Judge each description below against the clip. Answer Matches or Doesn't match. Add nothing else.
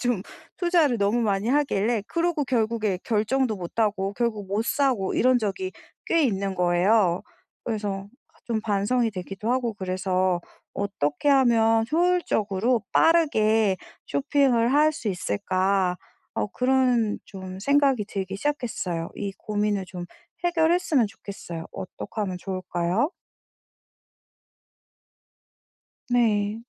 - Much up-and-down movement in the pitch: Doesn't match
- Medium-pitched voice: Doesn't match